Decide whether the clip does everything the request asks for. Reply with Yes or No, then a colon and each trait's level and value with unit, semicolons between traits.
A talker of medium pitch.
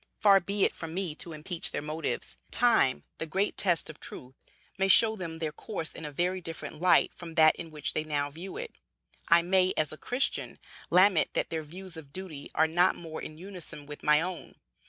Yes: medium, 165 Hz